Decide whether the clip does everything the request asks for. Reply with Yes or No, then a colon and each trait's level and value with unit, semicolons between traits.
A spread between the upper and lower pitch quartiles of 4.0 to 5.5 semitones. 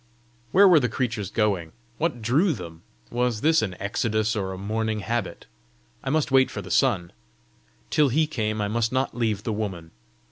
Yes: average, 4.4 semitones